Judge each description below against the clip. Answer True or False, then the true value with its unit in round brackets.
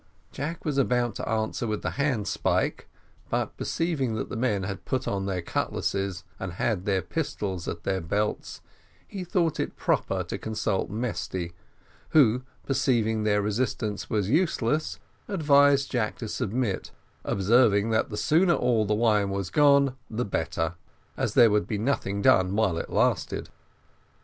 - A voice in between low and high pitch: False (110 Hz)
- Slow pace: False (155 wpm)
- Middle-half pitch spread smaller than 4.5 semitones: False (5.0 semitones)